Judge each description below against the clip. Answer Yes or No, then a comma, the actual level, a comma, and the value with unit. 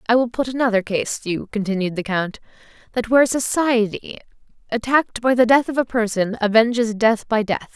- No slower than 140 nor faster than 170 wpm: No, average, 185 wpm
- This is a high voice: Yes, high, 230 Hz